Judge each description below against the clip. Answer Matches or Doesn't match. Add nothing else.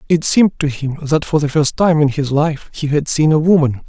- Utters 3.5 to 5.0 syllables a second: Doesn't match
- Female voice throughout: Doesn't match